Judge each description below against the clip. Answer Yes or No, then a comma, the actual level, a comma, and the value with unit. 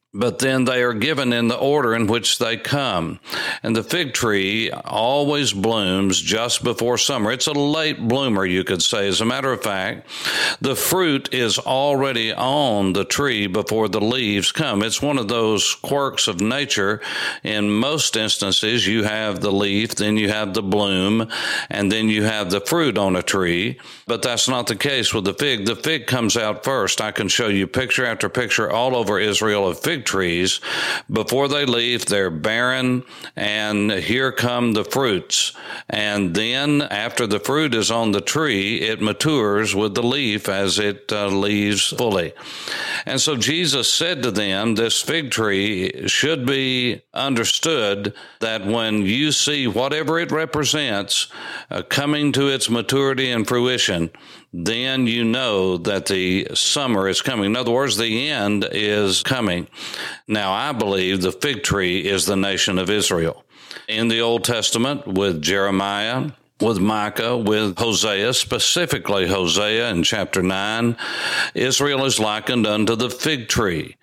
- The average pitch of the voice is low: Yes, low, 110 Hz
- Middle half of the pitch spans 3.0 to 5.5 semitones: Yes, average, 3.8 semitones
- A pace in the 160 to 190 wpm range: Yes, average, 165 wpm